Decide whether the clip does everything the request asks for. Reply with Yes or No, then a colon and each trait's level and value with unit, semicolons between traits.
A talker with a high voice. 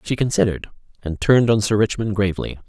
No: low, 105 Hz